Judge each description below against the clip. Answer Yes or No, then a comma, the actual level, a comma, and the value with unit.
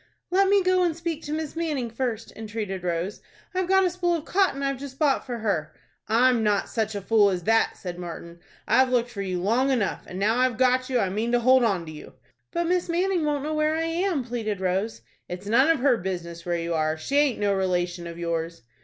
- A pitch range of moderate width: No, wide, 7.9 semitones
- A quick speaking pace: Yes, fast, 235 wpm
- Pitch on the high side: Yes, high, 235 Hz